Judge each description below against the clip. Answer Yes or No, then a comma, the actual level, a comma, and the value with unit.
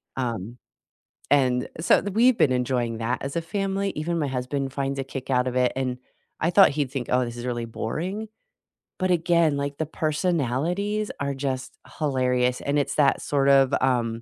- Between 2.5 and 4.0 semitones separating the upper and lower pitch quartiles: No, average, 4.5 semitones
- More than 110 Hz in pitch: Yes, medium, 140 Hz